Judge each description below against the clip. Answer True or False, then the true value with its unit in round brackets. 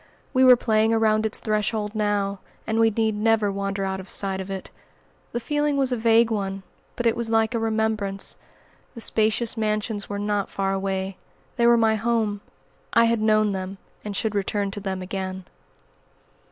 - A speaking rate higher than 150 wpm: True (180 wpm)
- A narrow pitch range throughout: True (2.3 semitones)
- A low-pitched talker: False (215 Hz)